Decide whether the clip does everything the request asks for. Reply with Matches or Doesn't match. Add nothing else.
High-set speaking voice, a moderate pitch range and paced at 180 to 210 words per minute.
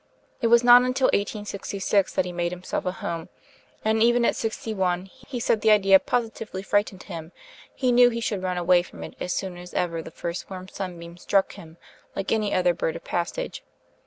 Matches